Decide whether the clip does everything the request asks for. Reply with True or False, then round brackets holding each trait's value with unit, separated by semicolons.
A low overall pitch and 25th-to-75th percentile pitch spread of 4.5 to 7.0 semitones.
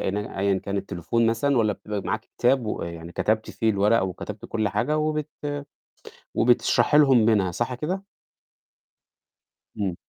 True (110 Hz; 5.1 semitones)